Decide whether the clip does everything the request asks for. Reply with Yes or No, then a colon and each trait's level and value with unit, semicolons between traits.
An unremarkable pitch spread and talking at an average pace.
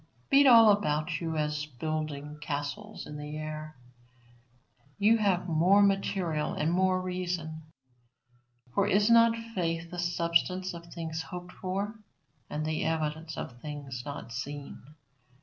No: average, 3.6 semitones; slow, 130 wpm